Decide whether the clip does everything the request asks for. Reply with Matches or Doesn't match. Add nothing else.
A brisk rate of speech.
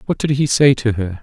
Matches